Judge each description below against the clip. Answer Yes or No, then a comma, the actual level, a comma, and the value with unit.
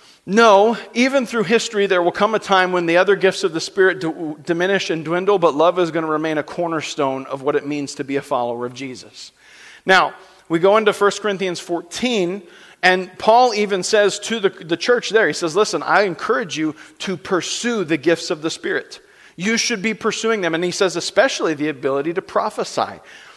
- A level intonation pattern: No, average, 4.6 semitones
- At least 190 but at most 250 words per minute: Yes, fast, 205 wpm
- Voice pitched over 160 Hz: Yes, medium, 185 Hz